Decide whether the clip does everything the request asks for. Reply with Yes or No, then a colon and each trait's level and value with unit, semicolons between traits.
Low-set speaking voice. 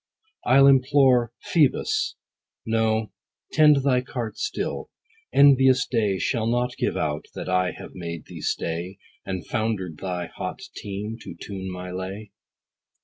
Yes: low, 110 Hz